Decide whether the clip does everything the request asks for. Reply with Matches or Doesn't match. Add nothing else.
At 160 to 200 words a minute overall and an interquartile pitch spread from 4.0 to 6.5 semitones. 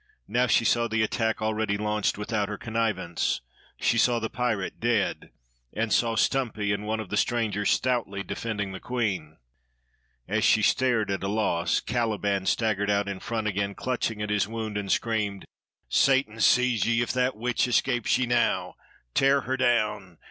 Doesn't match